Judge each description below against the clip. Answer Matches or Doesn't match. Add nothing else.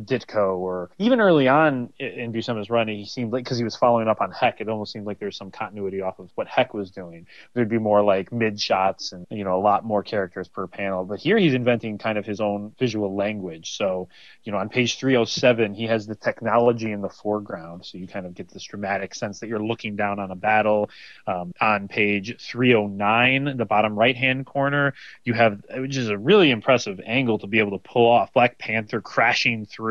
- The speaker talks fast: Matches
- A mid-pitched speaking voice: Doesn't match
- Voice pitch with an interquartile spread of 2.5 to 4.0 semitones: Matches